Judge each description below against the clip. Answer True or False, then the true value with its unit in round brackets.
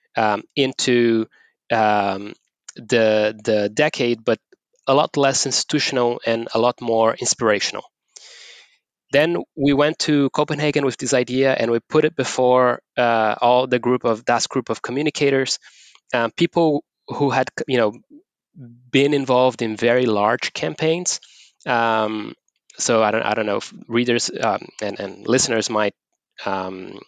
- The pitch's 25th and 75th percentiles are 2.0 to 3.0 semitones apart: False (3.8 semitones)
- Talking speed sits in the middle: True (145 wpm)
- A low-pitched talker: True (125 Hz)